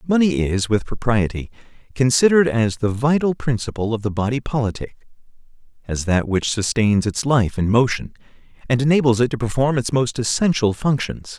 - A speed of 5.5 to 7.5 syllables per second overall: No, 5.3 syllables/s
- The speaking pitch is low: Yes, low, 120 Hz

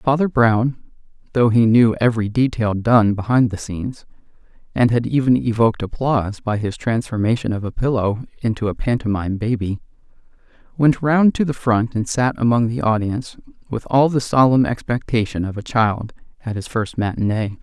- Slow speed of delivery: No, average, 165 wpm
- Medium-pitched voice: No, low, 115 Hz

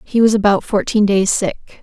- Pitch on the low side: No, high, 205 Hz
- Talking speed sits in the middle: Yes, average, 195 wpm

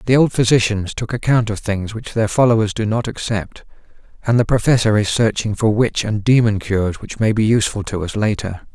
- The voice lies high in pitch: No, low, 110 Hz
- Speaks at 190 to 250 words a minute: Yes, fast, 205 wpm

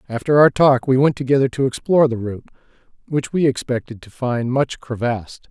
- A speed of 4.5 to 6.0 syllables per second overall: Yes, 5.8 syllables/s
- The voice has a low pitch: Yes, low, 130 Hz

